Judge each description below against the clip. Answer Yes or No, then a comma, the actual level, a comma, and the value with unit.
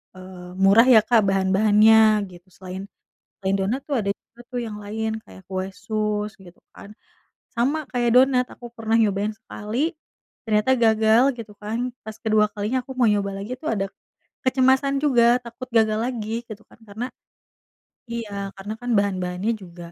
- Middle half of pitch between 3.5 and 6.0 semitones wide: No, average, 3.1 semitones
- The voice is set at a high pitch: Yes, high, 215 Hz